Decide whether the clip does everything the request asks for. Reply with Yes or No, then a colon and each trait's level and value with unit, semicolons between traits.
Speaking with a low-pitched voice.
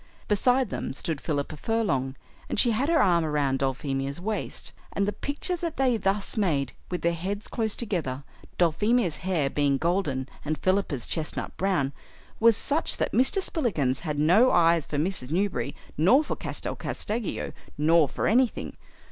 No: medium, 175 Hz